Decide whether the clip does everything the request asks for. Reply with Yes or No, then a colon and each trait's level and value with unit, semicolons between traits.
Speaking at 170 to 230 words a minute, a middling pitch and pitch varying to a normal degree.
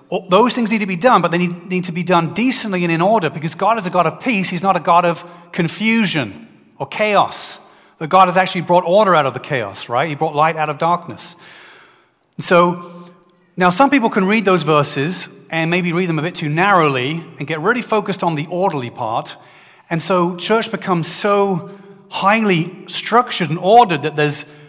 Yes: fast, 205 wpm; medium, 175 Hz; average, 3.4 semitones